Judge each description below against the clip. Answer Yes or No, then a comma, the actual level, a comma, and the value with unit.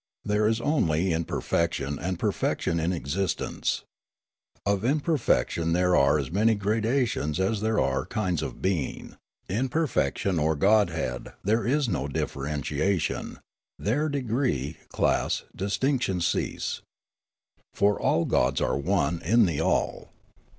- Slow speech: Yes, slow, 125 wpm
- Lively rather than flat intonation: Yes, wide, 6.2 semitones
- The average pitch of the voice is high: No, very low, 95 Hz